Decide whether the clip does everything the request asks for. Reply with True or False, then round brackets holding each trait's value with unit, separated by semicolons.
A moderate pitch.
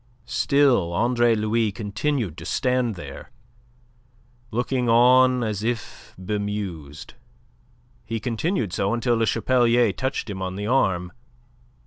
False (115 Hz)